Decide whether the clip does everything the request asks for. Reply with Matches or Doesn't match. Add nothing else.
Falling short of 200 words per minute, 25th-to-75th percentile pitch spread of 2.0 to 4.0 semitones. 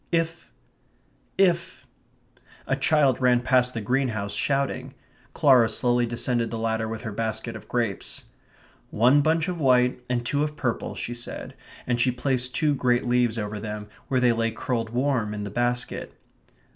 Matches